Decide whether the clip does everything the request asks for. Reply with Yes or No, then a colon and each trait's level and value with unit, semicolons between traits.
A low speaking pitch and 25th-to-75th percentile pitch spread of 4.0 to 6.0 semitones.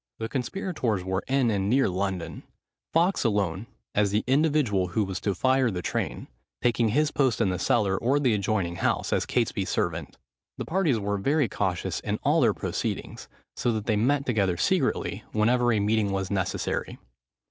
Yes: low, 110 Hz; average, 5.2 semitones